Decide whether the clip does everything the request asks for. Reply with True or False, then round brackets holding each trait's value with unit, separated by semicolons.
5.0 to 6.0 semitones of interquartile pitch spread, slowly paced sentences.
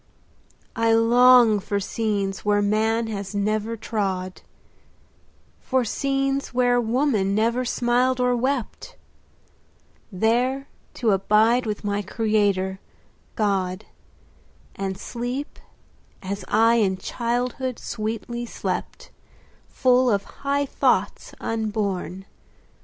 False (3.4 semitones; 100 wpm)